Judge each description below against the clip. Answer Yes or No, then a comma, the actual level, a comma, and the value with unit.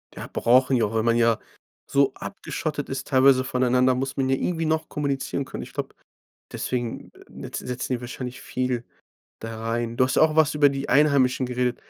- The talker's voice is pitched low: Yes, low, 130 Hz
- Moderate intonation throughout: No, narrow, 2.2 semitones